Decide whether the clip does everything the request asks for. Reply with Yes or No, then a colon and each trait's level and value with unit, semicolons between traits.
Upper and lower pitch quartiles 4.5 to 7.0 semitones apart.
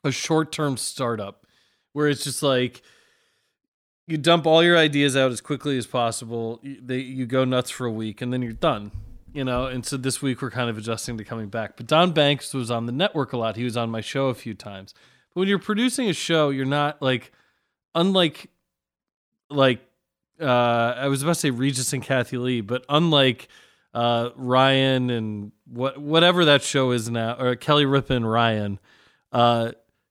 No: average, 3.7 semitones